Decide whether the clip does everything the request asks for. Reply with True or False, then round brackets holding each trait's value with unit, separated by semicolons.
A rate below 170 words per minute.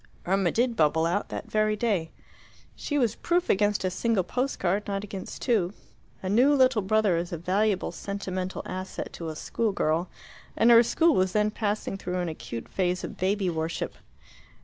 False (180 wpm)